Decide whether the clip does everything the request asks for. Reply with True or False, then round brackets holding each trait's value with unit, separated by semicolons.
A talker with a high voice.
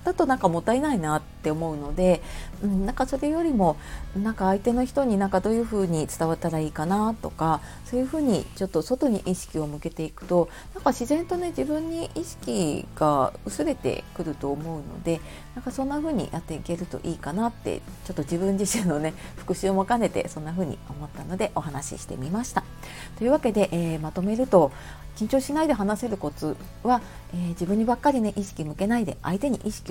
True (195 Hz)